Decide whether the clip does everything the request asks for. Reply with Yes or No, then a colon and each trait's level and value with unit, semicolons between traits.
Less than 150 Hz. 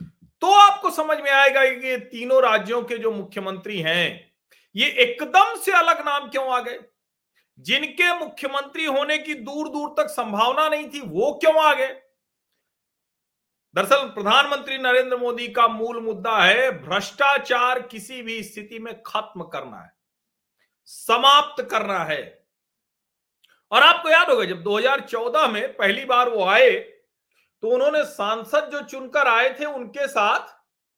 No: very high, 265 Hz